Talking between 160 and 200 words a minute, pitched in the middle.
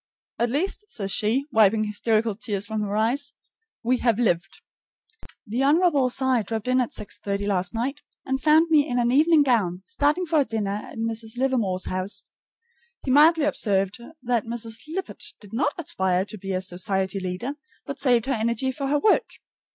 No: average, 175 wpm; high, 235 Hz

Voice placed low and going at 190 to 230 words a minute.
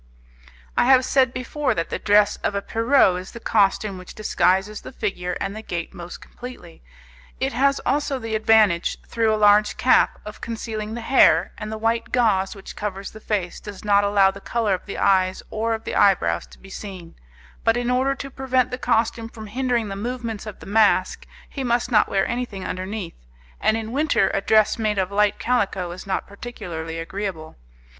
No: high, 215 Hz; average, 195 wpm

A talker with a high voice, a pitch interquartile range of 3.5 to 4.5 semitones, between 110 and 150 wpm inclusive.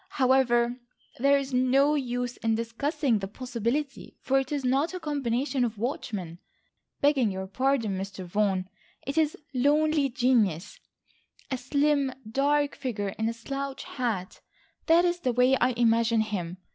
Yes: very high, 250 Hz; average, 3.8 semitones; average, 145 wpm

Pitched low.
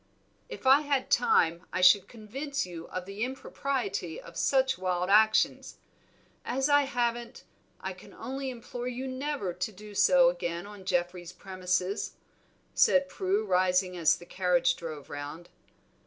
No: high, 205 Hz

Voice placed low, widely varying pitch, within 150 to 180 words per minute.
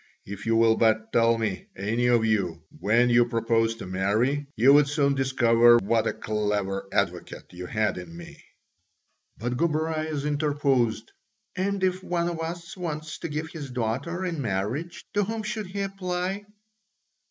Yes: low, 125 Hz; wide, 6.6 semitones; average, 160 wpm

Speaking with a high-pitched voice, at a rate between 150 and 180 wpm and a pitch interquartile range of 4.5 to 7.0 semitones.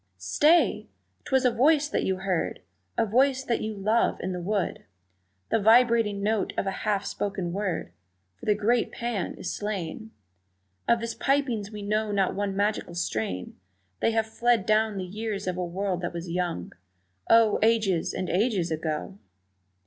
No: high, 205 Hz; average, 165 wpm; average, 3.7 semitones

